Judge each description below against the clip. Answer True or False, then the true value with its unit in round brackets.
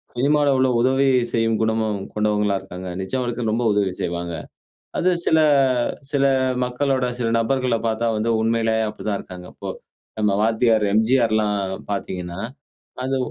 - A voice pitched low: True (110 Hz)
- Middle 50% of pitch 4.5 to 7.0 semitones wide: False (3.2 semitones)